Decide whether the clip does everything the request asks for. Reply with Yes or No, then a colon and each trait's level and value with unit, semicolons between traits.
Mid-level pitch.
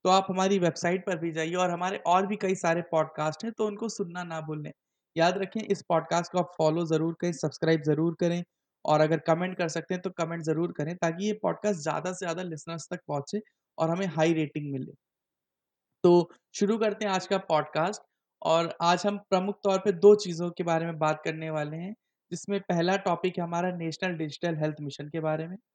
Yes: medium, 175 Hz